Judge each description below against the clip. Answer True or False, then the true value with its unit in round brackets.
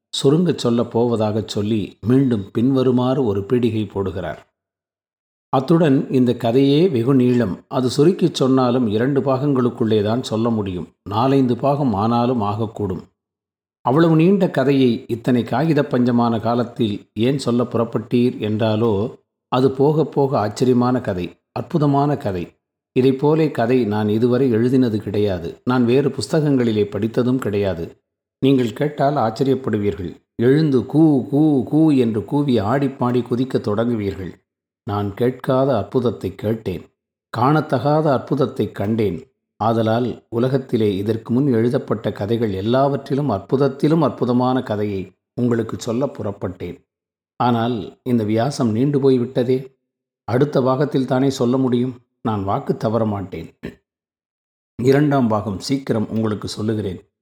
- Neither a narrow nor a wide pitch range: True (3.9 semitones)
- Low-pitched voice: True (120 Hz)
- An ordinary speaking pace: True (110 wpm)